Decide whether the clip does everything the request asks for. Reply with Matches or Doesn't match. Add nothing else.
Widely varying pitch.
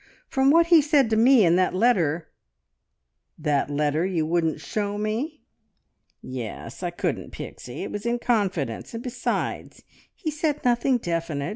Matches